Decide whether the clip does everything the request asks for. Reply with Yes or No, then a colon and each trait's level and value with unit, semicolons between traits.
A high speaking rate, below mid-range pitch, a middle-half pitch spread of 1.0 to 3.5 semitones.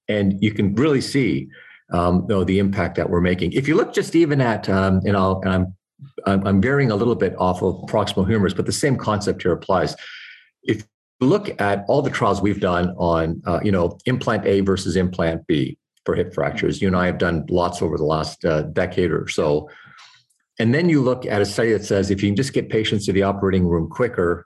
Yes: fast, 230 wpm; very low, 95 Hz; average, 2.9 semitones